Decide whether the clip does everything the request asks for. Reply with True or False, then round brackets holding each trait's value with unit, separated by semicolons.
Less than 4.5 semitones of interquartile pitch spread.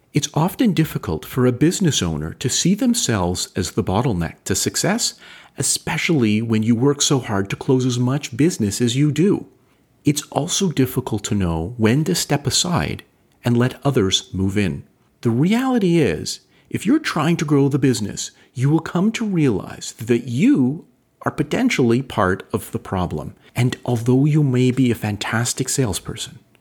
False (5.6 semitones)